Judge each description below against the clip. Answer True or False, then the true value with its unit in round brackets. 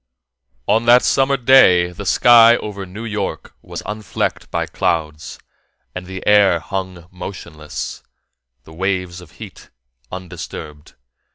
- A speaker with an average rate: False (120 wpm)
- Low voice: True (95 Hz)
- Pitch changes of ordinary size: True (3.5 semitones)